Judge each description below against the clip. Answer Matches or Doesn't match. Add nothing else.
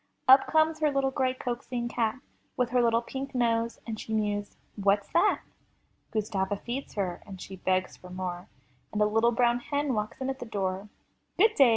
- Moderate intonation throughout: Matches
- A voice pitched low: Doesn't match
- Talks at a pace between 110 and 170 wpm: Doesn't match